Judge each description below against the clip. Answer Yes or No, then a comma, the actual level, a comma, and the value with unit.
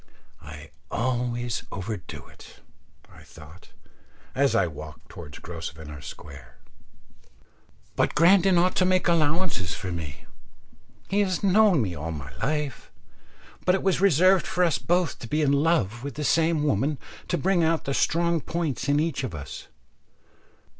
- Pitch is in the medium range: Yes, medium, 145 Hz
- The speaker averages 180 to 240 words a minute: No, average, 150 wpm